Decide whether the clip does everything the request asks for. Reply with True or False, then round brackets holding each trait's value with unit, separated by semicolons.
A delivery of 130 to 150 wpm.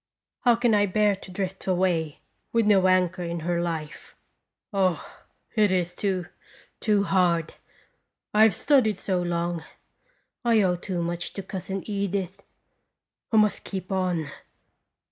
True (140 wpm)